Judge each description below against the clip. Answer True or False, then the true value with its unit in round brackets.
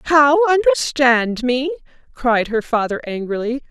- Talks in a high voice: True (270 Hz)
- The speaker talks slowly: True (115 wpm)